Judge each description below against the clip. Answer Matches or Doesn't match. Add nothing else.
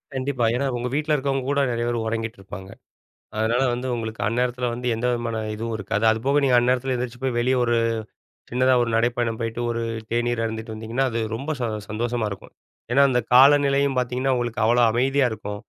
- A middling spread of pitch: Doesn't match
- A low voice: Matches